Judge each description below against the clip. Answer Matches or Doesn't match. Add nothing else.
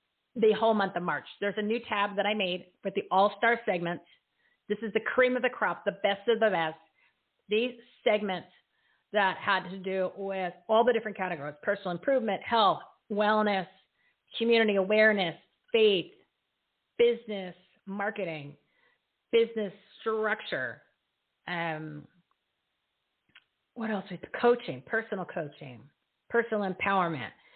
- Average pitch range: Matches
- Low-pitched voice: Doesn't match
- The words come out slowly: Matches